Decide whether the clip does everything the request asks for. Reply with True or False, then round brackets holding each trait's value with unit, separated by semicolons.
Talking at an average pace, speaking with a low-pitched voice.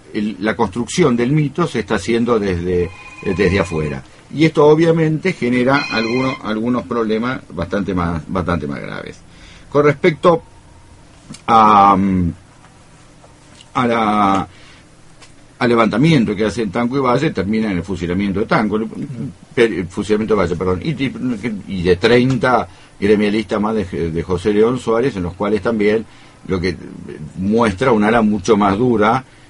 True (140 wpm; 110 Hz)